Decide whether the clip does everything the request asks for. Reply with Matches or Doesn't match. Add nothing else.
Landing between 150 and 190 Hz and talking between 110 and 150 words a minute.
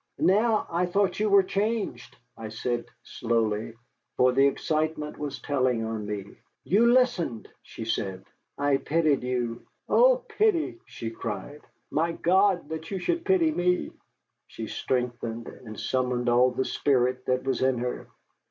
Doesn't match